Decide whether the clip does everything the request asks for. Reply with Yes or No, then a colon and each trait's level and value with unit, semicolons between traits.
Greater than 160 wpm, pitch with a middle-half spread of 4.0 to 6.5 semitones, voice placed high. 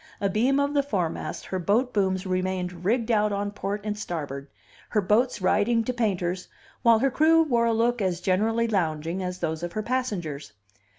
Yes: average, 180 wpm; average, 4.4 semitones; high, 205 Hz